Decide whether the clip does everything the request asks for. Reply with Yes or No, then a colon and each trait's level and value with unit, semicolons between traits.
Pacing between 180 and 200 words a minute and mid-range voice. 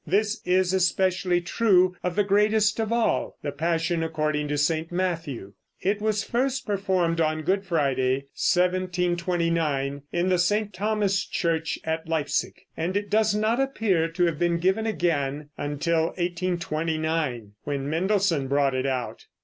No: average, 145 wpm; medium, 175 Hz